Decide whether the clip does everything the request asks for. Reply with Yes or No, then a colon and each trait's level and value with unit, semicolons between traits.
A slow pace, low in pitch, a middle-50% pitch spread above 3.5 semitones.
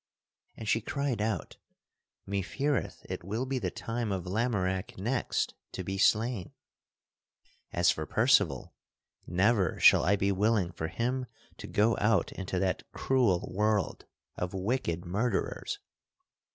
Yes: slow, 130 wpm; low, 100 Hz; average, 3.9 semitones